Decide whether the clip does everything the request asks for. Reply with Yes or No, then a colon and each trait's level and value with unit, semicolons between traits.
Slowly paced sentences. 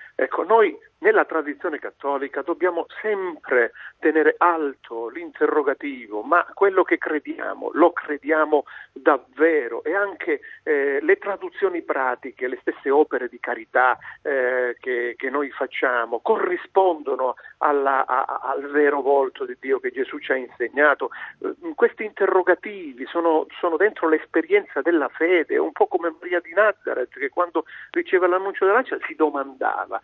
No: average, 140 wpm